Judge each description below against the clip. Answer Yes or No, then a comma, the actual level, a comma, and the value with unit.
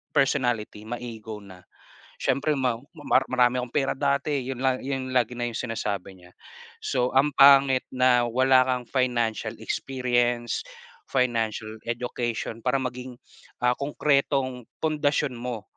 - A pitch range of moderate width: No, narrow, 2.1 semitones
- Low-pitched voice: Yes, low, 125 Hz